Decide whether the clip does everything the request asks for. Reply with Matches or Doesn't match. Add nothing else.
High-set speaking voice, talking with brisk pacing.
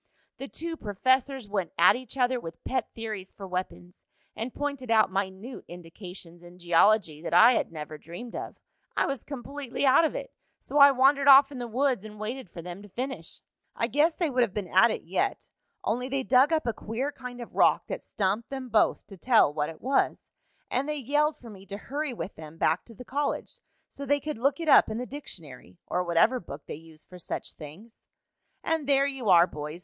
Matches